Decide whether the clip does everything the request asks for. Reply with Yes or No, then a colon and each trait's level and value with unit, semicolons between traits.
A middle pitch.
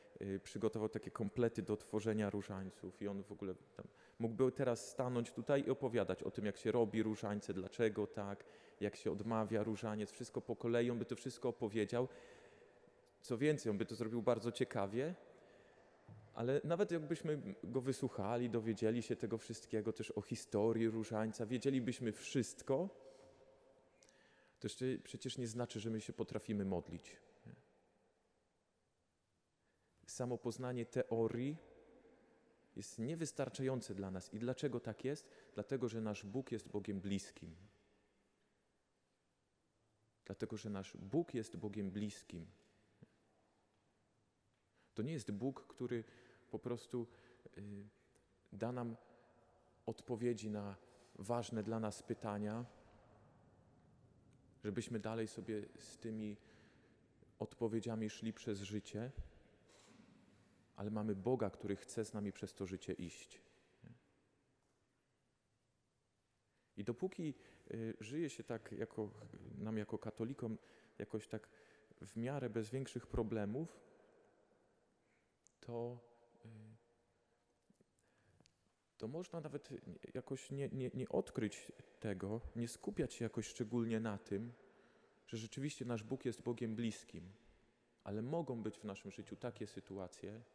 No: low, 115 Hz